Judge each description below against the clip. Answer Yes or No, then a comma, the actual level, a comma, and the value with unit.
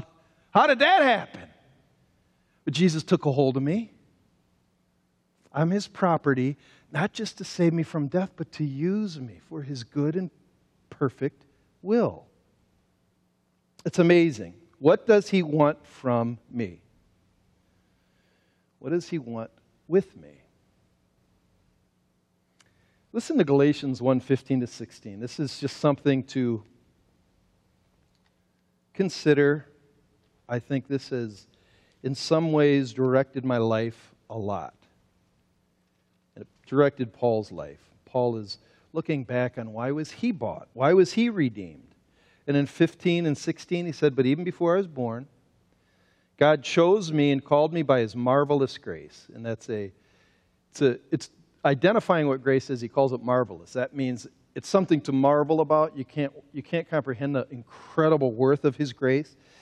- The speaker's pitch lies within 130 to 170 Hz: Yes, medium, 140 Hz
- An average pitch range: Yes, average, 4.7 semitones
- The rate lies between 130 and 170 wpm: Yes, average, 145 wpm